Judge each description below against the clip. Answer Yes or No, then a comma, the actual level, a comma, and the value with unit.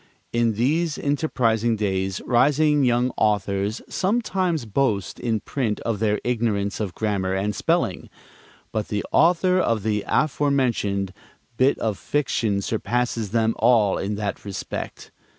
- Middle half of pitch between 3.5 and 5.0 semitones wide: Yes, average, 4.7 semitones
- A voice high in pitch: No, low, 115 Hz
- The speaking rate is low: Yes, slow, 130 wpm